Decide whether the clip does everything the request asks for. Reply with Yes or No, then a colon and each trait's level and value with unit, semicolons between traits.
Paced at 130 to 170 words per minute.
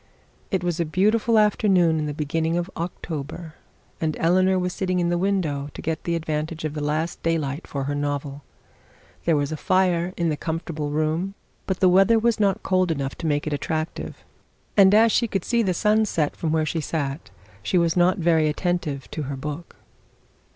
No: average, 195 wpm